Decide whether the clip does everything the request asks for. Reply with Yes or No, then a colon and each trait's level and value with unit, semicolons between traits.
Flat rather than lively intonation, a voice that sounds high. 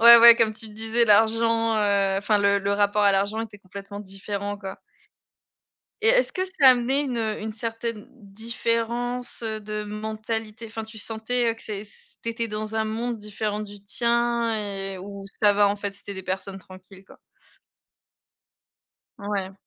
Yes: narrow, 2.2 semitones; high, 215 Hz